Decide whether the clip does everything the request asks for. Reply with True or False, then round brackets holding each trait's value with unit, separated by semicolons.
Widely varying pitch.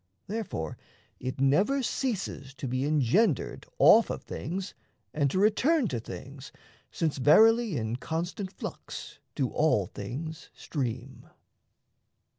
True (7.5 semitones)